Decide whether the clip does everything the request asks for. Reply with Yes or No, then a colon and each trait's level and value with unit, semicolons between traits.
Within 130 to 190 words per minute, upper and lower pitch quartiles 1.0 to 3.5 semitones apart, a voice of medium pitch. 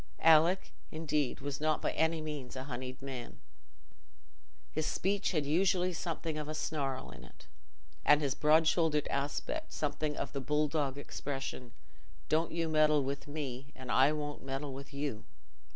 Yes: average, 155 wpm; narrow, 2.5 semitones; medium, 150 Hz